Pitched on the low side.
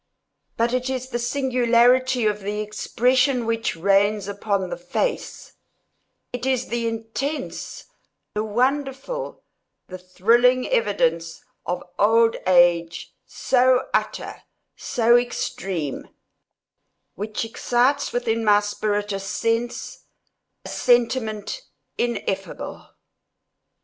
No: high, 230 Hz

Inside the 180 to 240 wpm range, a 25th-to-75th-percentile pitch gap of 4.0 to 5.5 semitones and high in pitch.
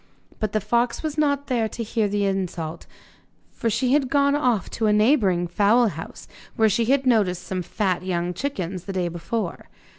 Yes: average, 185 wpm; average, 5.1 semitones; high, 215 Hz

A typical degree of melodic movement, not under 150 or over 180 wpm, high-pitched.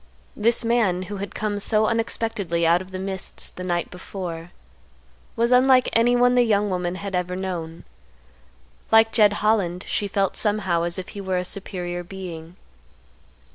Yes: average, 3.4 semitones; average, 160 wpm; high, 195 Hz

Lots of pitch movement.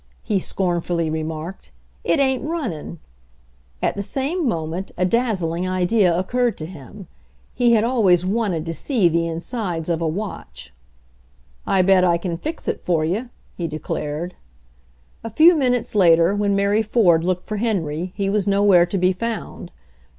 No: average, 4.7 semitones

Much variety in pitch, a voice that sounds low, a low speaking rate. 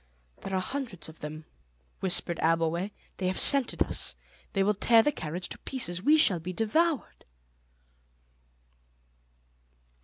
No: wide, 5.7 semitones; high, 190 Hz; slow, 130 wpm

